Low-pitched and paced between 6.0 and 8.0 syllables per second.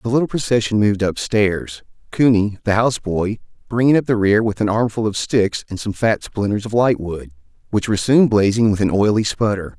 No: low, 105 Hz; 5.3 syllables/s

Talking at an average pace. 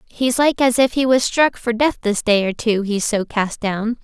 No: fast, 240 wpm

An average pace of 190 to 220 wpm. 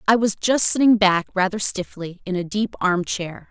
Yes: fast, 205 wpm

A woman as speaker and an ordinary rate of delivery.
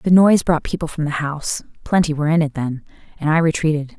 Yes: female; average, 195 wpm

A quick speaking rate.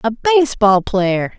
No: average, 175 wpm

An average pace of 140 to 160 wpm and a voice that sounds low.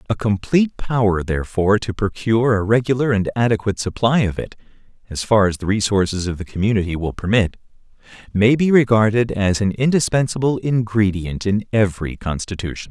Yes: average, 155 wpm; low, 105 Hz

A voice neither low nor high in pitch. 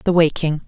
Yes: medium, 160 Hz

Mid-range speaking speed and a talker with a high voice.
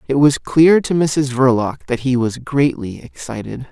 No: average, 180 wpm; low, 135 Hz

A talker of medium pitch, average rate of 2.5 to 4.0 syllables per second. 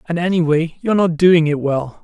No: medium, 165 Hz; 5.3 syllables/s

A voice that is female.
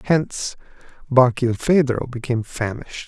No: male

